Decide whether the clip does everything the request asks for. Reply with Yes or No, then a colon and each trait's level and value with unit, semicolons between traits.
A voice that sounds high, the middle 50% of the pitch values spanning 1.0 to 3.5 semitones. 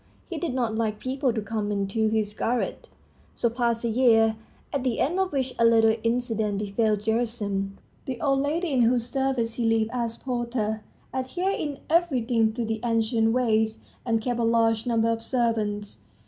Yes: high, 230 Hz; narrow, 2.4 semitones